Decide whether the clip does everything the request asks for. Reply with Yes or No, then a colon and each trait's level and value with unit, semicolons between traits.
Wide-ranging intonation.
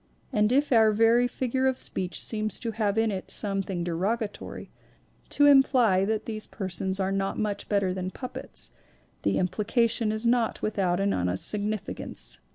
No: average, 3.2 semitones